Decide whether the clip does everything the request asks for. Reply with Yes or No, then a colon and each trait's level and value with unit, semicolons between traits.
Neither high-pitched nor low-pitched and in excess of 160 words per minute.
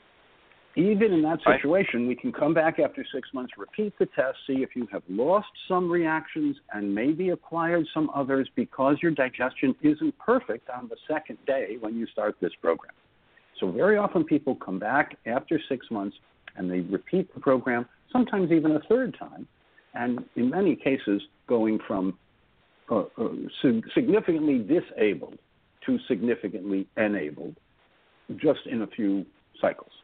No: medium, 145 Hz; average, 150 wpm